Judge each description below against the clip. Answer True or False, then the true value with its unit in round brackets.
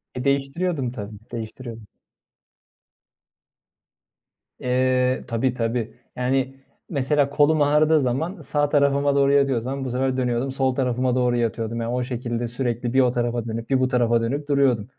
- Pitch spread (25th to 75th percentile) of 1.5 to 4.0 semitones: True (2.6 semitones)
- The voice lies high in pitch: False (130 Hz)